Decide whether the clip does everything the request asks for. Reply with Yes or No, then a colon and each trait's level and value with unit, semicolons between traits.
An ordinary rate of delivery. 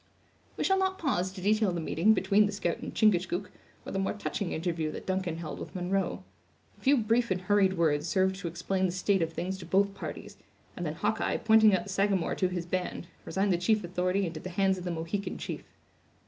No: fast, 220 wpm